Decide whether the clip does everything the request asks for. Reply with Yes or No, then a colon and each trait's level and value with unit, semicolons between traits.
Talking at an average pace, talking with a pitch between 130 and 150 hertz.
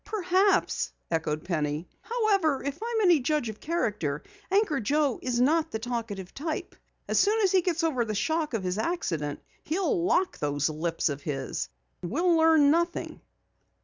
No: average, 160 wpm; very high, 290 Hz